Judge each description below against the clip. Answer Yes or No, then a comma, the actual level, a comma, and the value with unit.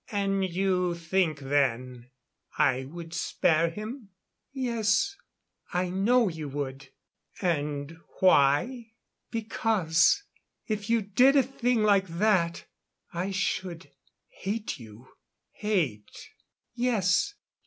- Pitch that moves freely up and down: Yes, wide, 5.9 semitones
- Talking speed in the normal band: No, slow, 100 wpm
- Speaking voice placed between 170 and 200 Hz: Yes, medium, 185 Hz